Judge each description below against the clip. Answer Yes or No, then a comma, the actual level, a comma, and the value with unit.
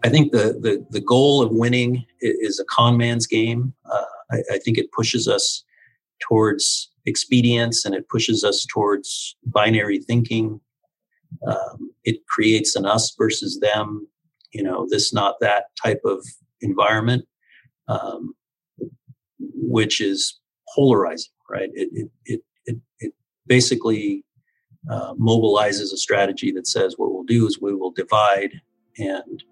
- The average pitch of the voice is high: No, low, 115 Hz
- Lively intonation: No, average, 3.3 semitones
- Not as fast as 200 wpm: Yes, average, 140 wpm